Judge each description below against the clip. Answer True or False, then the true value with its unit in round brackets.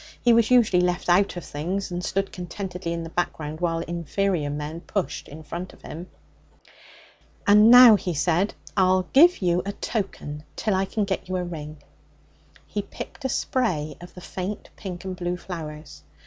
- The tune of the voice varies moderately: True (3.1 semitones)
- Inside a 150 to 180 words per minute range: True (175 wpm)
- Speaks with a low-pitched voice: False (180 Hz)